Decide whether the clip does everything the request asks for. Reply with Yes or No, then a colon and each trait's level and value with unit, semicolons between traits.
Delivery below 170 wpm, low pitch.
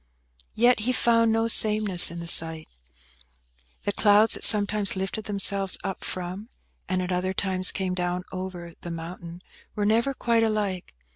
No: average, 155 wpm; high, 195 Hz